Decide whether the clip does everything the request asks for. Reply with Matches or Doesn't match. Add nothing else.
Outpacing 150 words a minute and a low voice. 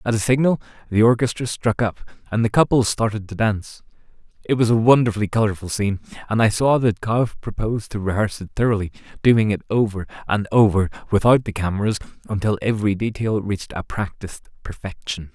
Matches